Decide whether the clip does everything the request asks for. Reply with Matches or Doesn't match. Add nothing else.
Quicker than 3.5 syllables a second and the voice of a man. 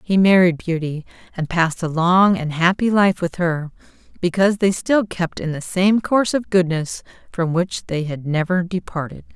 Doesn't match